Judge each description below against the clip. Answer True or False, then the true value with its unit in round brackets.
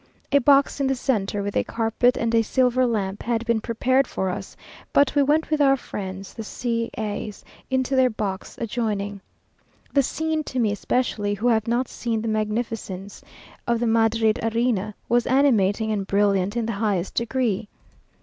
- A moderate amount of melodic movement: True (3.4 semitones)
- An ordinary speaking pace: True (175 wpm)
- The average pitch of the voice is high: True (230 Hz)